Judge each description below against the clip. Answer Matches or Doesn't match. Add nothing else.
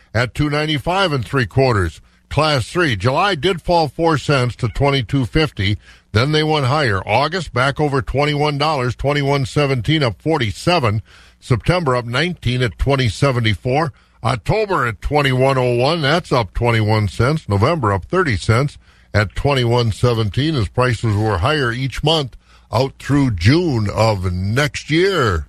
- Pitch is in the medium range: Doesn't match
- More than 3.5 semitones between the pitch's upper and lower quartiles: Matches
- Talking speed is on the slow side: Matches